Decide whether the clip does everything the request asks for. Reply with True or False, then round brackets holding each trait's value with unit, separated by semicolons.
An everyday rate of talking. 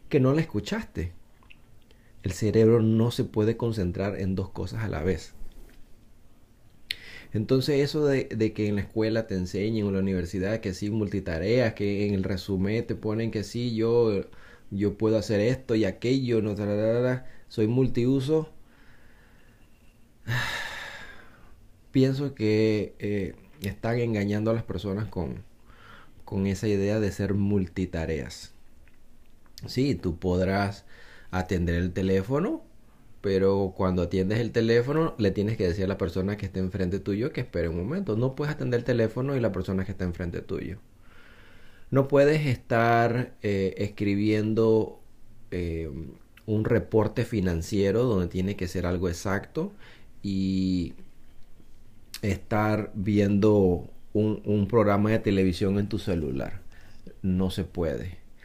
True (140 wpm)